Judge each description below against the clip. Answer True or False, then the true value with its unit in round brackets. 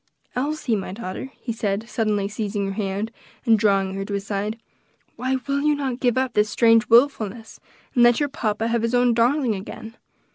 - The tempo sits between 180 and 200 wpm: True (190 wpm)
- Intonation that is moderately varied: True (3.3 semitones)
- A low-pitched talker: False (225 Hz)